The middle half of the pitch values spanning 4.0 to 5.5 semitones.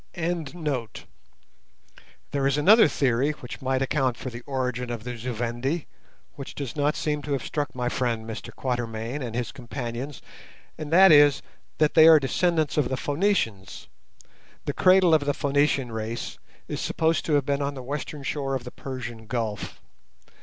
No: average, 3.4 semitones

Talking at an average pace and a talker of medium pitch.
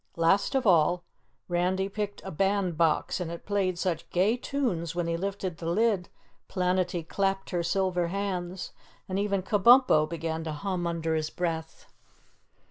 Yes: average, 155 wpm; medium, 180 Hz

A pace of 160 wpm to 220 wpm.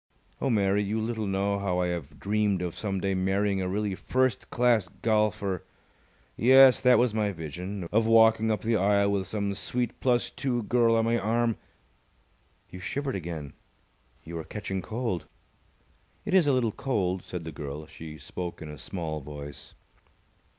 Yes: average, 170 wpm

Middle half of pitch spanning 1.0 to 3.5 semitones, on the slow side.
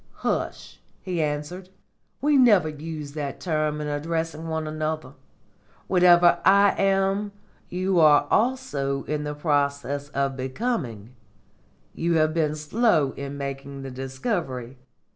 No: average, 4.1 semitones; slow, 120 wpm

